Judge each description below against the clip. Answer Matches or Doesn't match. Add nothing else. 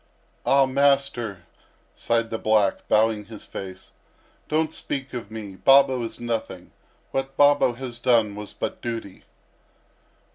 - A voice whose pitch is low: Matches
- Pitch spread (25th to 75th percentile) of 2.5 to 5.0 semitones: Matches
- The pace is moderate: Doesn't match